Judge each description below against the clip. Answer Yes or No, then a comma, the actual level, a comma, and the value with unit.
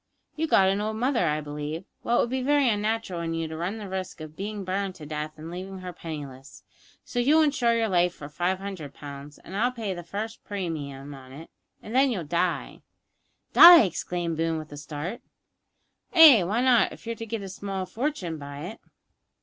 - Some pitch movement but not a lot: No, wide, 6.1 semitones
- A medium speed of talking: No, fast, 210 wpm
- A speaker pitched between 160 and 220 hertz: Yes, medium, 185 Hz